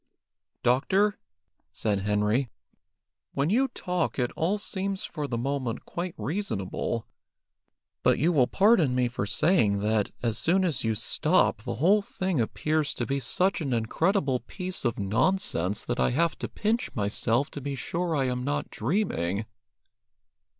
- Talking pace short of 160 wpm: Yes, average, 150 wpm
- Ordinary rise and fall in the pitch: No, wide, 8.0 semitones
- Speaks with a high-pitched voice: No, medium, 140 Hz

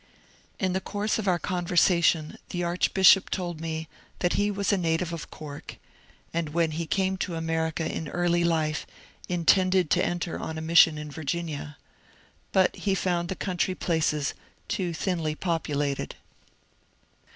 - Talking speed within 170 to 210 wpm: No, average, 150 wpm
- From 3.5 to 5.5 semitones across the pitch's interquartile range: No, narrow, 2.4 semitones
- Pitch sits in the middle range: Yes, medium, 170 Hz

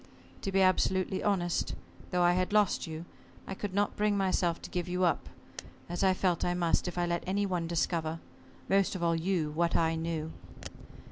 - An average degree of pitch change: No, narrow, 2.2 semitones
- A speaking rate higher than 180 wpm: Yes, average, 195 wpm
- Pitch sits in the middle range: Yes, medium, 180 Hz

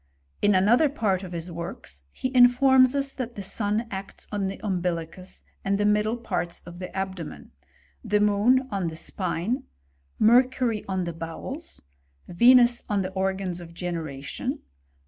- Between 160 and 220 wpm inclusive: No, average, 150 wpm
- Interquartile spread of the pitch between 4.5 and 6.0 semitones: Yes, average, 5.1 semitones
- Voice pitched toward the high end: Yes, high, 195 Hz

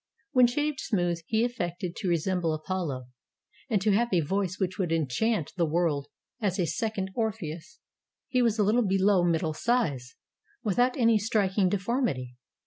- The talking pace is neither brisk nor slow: Yes, average, 160 wpm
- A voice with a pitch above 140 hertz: Yes, high, 190 Hz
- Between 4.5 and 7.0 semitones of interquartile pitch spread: Yes, average, 5.0 semitones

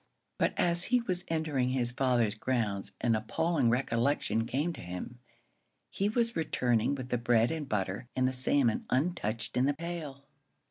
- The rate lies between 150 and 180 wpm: Yes, average, 165 wpm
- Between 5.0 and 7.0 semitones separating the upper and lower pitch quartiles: Yes, wide, 5.4 semitones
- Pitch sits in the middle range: No, low, 130 Hz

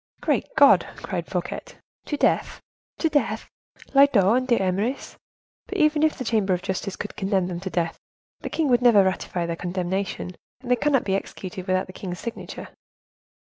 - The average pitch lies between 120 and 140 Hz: No, high, 195 Hz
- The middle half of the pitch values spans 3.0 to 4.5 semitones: No, wide, 5.6 semitones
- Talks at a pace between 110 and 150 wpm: No, average, 175 wpm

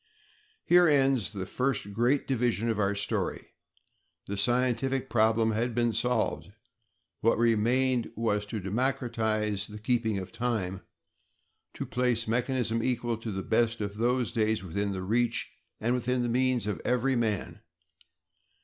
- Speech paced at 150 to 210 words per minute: No, average, 140 wpm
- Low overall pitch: Yes, low, 115 Hz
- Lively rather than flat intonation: No, average, 2.7 semitones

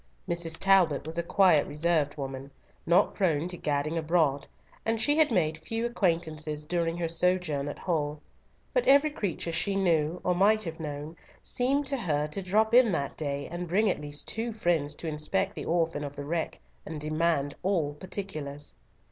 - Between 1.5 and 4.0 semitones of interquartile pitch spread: No, average, 4.4 semitones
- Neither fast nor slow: Yes, average, 180 wpm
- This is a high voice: No, medium, 165 Hz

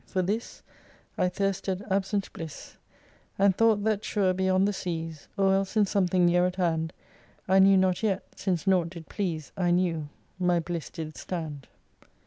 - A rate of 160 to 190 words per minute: Yes, average, 165 wpm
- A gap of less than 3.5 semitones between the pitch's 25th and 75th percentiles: Yes, narrow, 2.4 semitones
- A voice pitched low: No, medium, 185 Hz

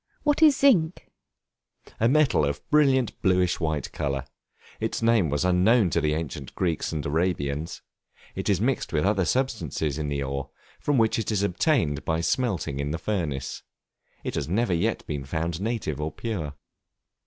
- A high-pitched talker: No, very low, 85 Hz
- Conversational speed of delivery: Yes, average, 170 wpm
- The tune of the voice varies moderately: No, wide, 7.4 semitones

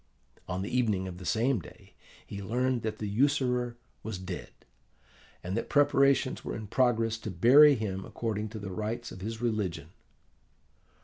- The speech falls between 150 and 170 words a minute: Yes, average, 165 wpm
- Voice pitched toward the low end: Yes, low, 110 Hz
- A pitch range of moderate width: Yes, average, 3.9 semitones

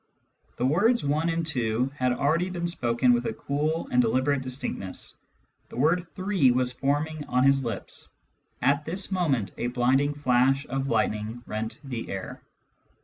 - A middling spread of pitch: Yes, average, 4.1 semitones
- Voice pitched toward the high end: No, low, 135 Hz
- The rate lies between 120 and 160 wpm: Yes, average, 155 wpm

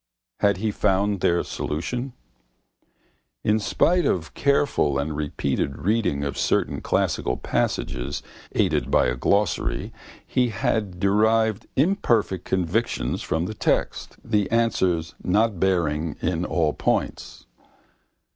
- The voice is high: No, very low, 95 Hz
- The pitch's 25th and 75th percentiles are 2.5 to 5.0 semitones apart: No, wide, 5.5 semitones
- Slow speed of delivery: Yes, slow, 115 wpm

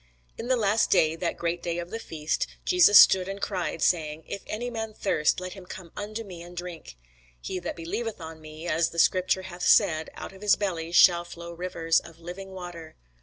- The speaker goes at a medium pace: No, fast, 210 wpm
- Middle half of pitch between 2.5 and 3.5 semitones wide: Yes, average, 2.9 semitones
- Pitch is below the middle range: No, medium, 175 Hz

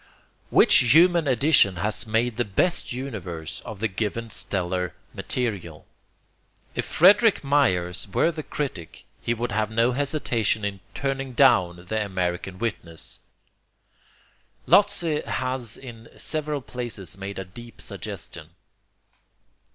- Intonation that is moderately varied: No, wide, 5.9 semitones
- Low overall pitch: Yes, low, 115 Hz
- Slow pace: Yes, slow, 120 wpm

